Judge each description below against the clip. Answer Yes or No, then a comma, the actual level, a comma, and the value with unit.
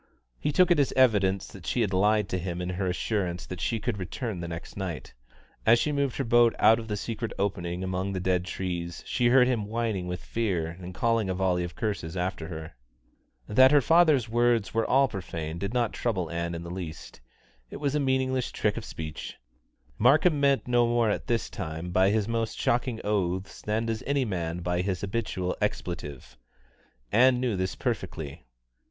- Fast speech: No, average, 195 wpm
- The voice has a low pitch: Yes, low, 100 Hz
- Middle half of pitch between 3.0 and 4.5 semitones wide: No, average, 5.0 semitones